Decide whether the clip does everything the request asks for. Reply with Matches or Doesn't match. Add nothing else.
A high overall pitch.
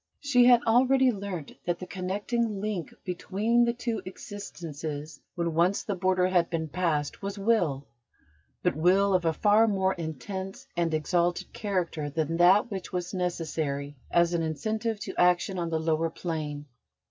Doesn't match